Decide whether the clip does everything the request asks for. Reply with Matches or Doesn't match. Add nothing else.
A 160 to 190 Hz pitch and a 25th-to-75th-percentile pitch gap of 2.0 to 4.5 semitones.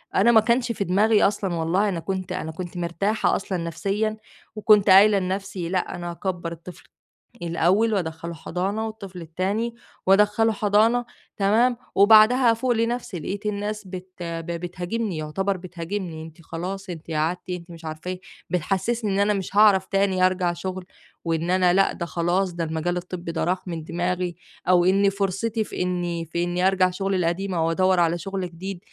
Matches